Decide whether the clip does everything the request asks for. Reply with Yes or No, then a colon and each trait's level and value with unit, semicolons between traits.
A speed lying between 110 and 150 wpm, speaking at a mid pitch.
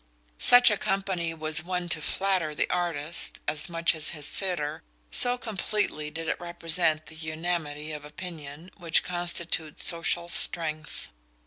Yes: slow, 135 wpm; medium, 165 Hz